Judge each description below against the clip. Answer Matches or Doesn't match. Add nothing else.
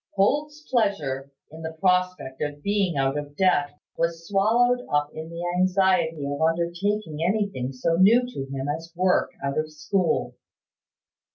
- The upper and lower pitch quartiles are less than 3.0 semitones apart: Doesn't match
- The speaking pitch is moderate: Matches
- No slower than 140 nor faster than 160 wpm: Matches